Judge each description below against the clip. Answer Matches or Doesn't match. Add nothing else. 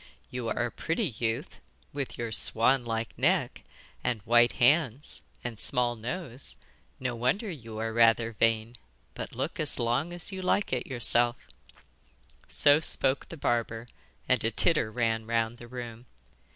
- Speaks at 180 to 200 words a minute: Doesn't match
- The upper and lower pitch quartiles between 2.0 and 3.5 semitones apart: Matches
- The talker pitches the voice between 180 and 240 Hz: Doesn't match